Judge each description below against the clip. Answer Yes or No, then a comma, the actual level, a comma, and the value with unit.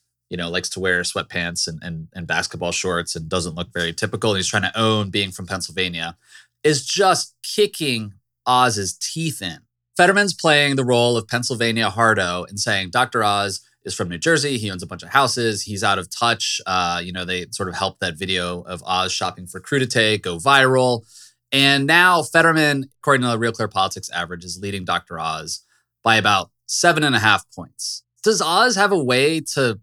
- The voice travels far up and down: Yes, wide, 6.3 semitones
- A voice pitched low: Yes, low, 110 Hz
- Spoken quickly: No, average, 195 wpm